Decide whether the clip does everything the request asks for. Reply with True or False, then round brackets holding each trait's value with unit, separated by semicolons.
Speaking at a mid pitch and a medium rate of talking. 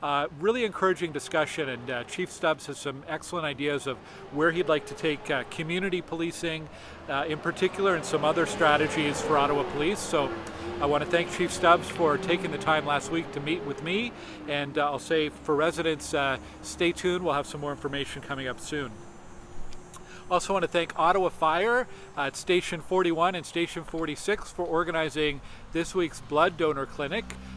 True (160 Hz; 185 wpm)